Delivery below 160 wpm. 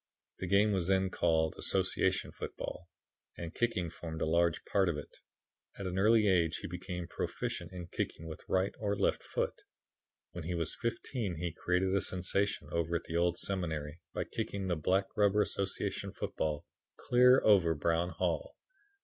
No: average, 165 wpm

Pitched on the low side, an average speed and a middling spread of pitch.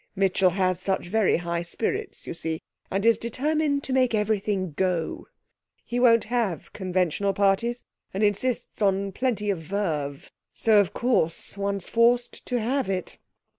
No: high, 200 Hz; average, 150 wpm; average, 4.2 semitones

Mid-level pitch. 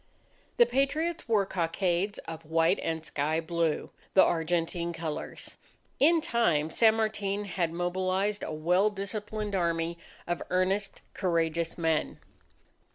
Yes: medium, 175 Hz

